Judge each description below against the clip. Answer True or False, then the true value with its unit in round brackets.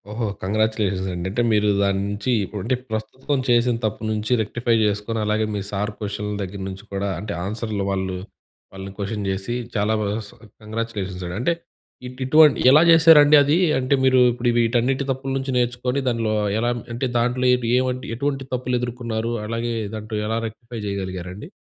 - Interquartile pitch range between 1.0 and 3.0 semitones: False (3.5 semitones)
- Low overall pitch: True (115 Hz)